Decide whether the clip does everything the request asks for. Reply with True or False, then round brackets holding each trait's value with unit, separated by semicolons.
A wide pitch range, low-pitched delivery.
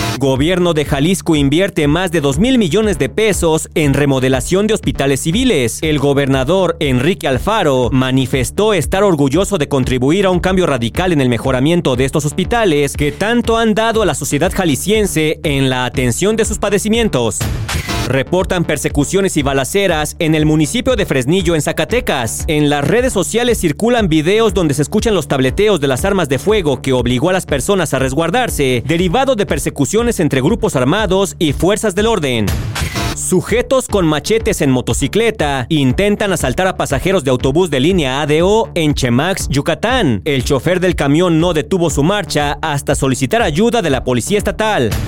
False (6.2 semitones; 160 Hz)